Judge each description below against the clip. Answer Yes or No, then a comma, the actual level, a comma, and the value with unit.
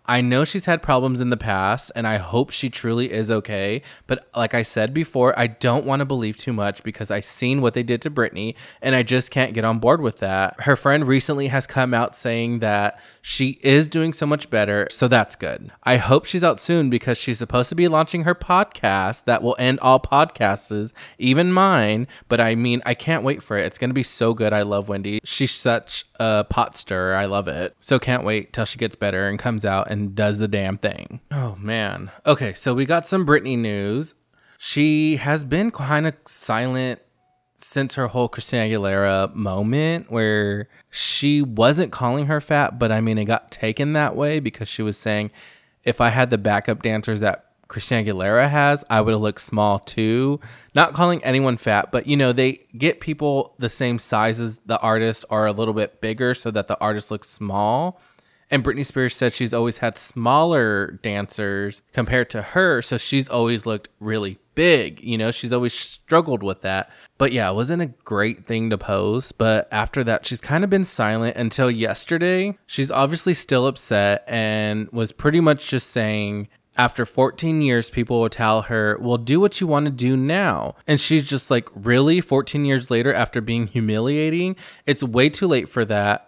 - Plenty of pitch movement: No, average, 4.2 semitones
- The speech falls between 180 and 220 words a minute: Yes, average, 200 wpm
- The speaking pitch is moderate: No, low, 120 Hz